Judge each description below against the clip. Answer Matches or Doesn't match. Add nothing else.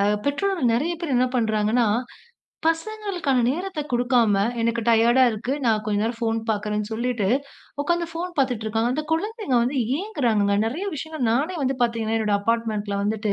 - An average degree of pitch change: Doesn't match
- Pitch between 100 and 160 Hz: Doesn't match